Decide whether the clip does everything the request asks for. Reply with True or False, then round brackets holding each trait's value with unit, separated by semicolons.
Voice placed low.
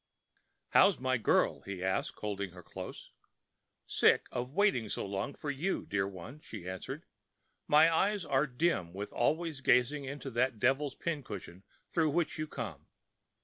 True (130 Hz)